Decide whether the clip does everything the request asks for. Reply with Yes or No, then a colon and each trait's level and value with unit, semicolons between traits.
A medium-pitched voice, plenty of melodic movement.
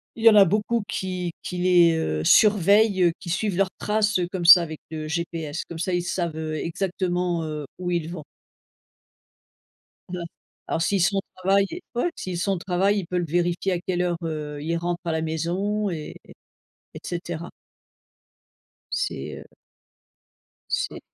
No: medium, 175 Hz; average, 2.7 semitones